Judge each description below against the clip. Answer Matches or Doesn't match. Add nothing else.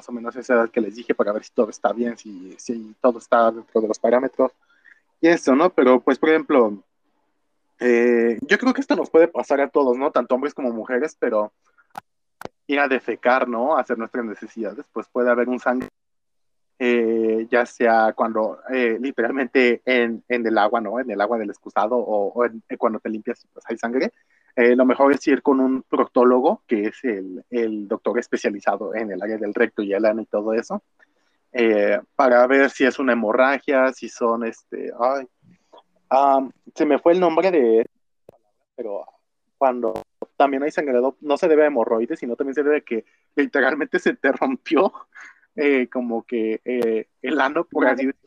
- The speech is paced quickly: Matches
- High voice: Doesn't match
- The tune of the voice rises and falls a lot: Doesn't match